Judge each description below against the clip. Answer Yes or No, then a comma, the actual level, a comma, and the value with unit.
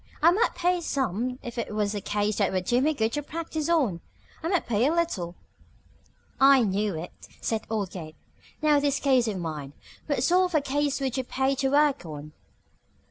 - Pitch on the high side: Yes, very high, 255 Hz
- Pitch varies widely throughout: Yes, wide, 6.3 semitones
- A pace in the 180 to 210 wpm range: Yes, average, 200 wpm